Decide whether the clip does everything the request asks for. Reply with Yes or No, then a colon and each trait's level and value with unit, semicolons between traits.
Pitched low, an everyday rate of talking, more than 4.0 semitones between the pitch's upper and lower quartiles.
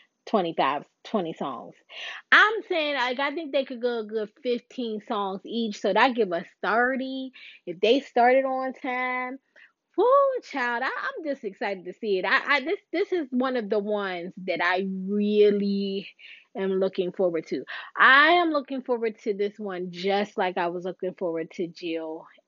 No: high, 225 Hz; average, 175 wpm; wide, 5.6 semitones